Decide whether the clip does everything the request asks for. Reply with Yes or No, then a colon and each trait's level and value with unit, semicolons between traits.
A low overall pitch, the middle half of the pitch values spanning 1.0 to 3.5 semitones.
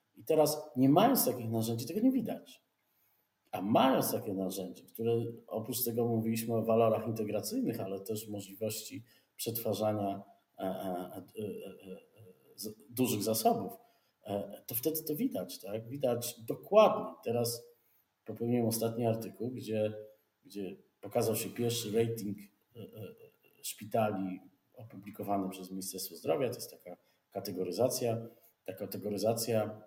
Yes: low, 115 Hz; narrow, 2.5 semitones